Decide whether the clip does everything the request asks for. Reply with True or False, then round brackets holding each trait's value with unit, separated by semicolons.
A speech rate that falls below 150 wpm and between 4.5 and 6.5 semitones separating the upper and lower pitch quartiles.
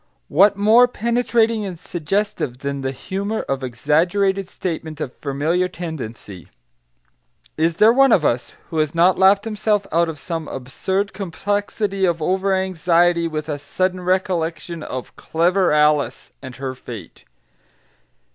True (135 wpm; 4.8 semitones)